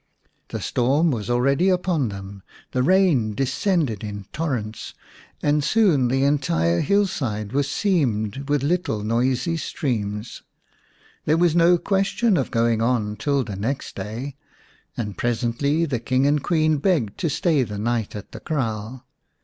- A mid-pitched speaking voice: No, low, 130 Hz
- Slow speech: No, average, 145 wpm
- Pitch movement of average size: No, wide, 6.3 semitones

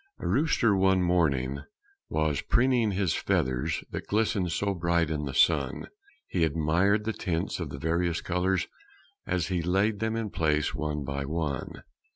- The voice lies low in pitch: Yes, very low, 85 Hz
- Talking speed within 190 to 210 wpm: No, average, 160 wpm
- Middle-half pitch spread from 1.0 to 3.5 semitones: No, average, 4.3 semitones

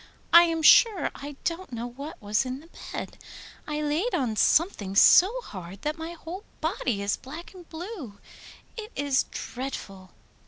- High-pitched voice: Yes, very high, 295 Hz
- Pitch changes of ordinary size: No, wide, 6.3 semitones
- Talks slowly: No, average, 160 wpm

